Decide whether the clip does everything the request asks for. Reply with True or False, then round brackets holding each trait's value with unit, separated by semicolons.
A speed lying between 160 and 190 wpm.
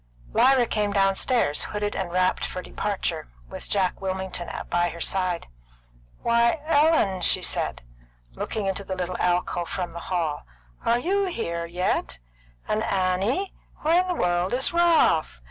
False (145 wpm)